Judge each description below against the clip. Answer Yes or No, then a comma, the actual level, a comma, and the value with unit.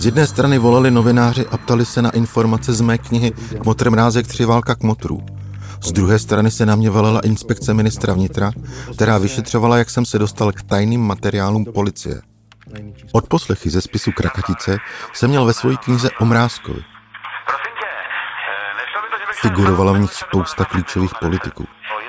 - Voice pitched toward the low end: Yes, low, 110 Hz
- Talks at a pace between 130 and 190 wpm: Yes, average, 155 wpm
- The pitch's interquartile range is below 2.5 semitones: No, average, 2.8 semitones